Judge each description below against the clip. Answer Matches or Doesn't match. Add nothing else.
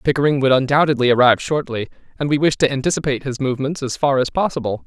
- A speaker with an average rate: Matches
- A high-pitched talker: Doesn't match